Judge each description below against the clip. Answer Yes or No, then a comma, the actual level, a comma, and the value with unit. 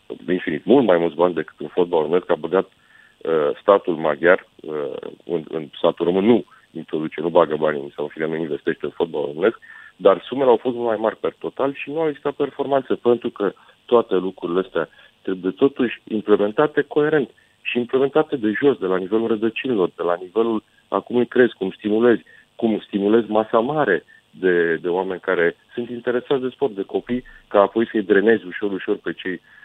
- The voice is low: Yes, low, 125 Hz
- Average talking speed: No, fast, 190 wpm